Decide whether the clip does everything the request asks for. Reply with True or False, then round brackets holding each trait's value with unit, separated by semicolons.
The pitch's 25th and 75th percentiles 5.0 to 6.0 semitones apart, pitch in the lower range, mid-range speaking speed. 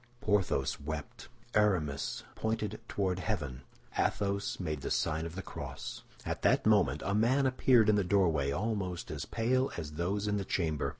True (5.3 semitones; 95 Hz; 165 wpm)